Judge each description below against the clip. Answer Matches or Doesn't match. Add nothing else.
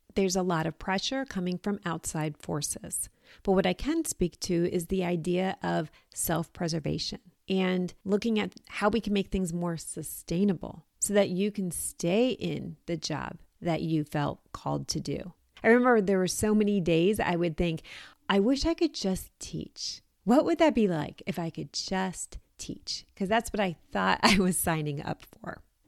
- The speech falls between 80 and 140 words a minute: Doesn't match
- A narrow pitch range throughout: Doesn't match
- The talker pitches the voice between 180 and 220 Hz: Matches